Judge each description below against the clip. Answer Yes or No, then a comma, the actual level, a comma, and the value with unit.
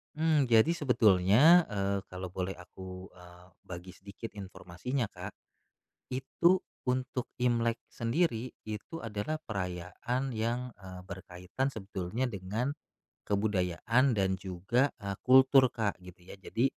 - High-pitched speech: No, low, 110 Hz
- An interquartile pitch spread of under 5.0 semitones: No, wide, 5.4 semitones